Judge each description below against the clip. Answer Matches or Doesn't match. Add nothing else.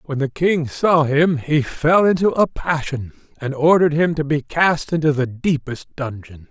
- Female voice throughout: Doesn't match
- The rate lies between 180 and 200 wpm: Matches